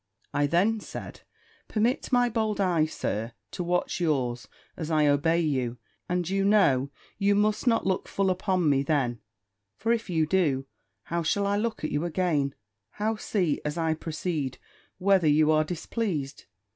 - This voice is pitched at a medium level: Yes, medium, 170 Hz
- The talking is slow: No, average, 165 wpm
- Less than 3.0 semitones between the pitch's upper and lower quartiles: No, average, 5.1 semitones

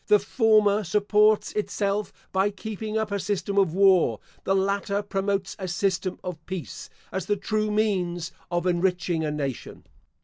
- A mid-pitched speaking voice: No, high, 195 Hz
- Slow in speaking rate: No, average, 150 wpm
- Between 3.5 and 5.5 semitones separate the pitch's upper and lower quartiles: No, narrow, 2.4 semitones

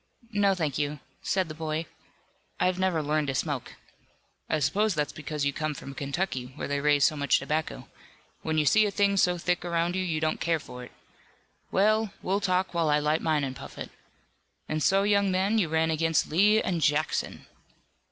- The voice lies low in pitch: No, medium, 160 Hz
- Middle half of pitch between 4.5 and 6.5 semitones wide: No, average, 4.0 semitones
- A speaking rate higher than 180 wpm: Yes, average, 195 wpm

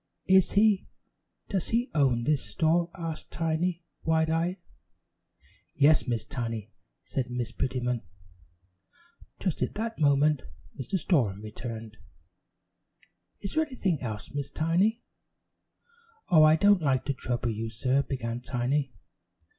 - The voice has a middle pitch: Yes, medium, 145 Hz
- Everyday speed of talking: No, slow, 125 wpm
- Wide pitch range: Yes, wide, 6.0 semitones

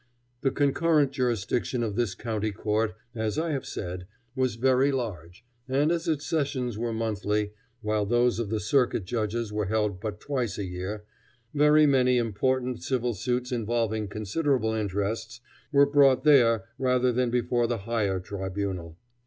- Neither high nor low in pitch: No, low, 115 Hz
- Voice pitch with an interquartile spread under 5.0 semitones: Yes, average, 3.7 semitones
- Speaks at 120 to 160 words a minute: Yes, average, 155 wpm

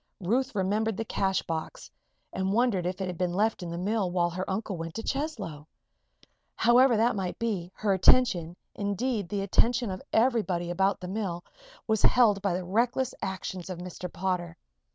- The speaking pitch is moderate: No, high, 195 Hz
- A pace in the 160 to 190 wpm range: Yes, average, 175 wpm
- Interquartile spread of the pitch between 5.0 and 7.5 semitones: No, average, 3.9 semitones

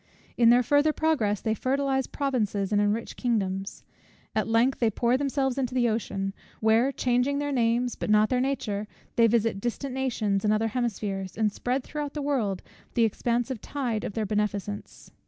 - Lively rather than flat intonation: No, average, 3.8 semitones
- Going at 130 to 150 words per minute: No, average, 175 wpm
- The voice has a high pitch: Yes, high, 235 Hz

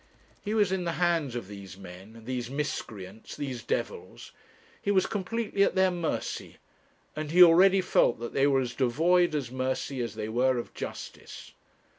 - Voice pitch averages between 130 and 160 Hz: Yes, medium, 140 Hz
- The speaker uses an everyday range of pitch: No, wide, 7.2 semitones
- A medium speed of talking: Yes, average, 170 wpm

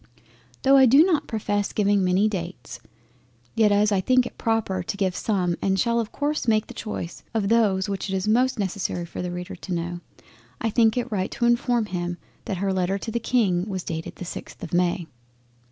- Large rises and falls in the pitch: No, average, 3.9 semitones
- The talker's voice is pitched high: Yes, high, 205 Hz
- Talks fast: Yes, fast, 210 wpm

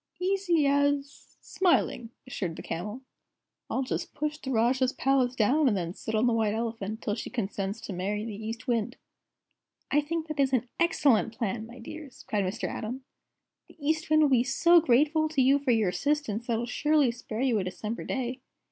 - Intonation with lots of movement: No, average, 4.7 semitones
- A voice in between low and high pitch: No, very high, 250 Hz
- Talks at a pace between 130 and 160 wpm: No, average, 190 wpm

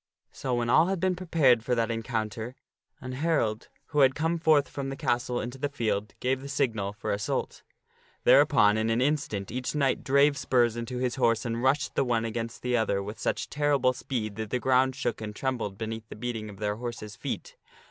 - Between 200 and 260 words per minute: Yes, fast, 205 wpm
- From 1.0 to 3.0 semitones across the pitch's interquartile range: No, average, 3.4 semitones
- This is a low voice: Yes, low, 120 Hz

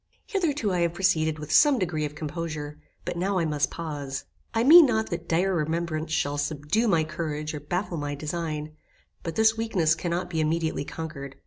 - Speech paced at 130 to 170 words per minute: No, average, 185 wpm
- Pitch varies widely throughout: No, average, 3.3 semitones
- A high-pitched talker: No, medium, 165 Hz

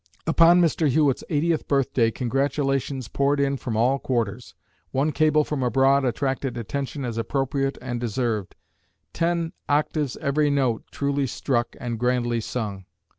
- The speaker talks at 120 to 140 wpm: Yes, slow, 135 wpm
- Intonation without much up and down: No, average, 3.0 semitones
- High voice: No, low, 135 Hz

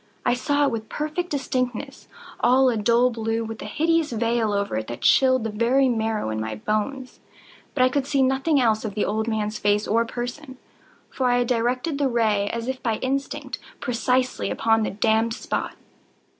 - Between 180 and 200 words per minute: Yes, average, 185 wpm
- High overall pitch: Yes, high, 240 Hz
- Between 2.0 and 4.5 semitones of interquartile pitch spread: Yes, average, 3.2 semitones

